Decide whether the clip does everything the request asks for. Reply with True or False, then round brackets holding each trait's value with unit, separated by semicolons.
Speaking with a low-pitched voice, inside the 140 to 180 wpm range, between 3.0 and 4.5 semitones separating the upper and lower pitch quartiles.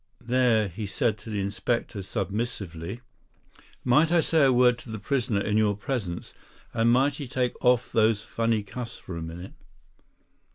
True (115 Hz; 165 wpm; 3.7 semitones)